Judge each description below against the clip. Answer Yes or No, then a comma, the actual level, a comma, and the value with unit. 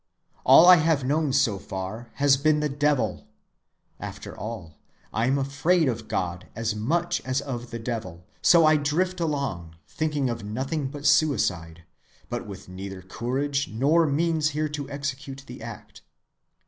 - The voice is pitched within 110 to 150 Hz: Yes, low, 135 Hz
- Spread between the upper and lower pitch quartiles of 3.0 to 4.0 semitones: No, average, 5.3 semitones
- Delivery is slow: No, average, 155 wpm